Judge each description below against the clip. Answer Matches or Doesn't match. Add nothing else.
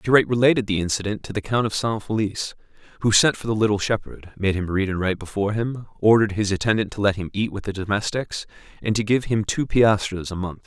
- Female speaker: Doesn't match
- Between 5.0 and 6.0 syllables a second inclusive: Doesn't match